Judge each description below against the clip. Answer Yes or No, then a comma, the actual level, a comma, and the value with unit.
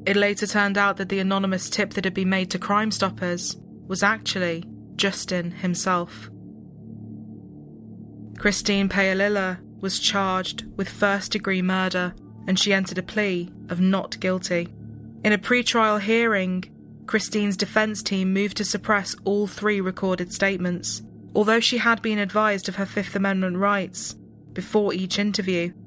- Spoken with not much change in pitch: Yes, narrow, 1.8 semitones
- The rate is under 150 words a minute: Yes, average, 140 wpm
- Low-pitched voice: No, high, 195 Hz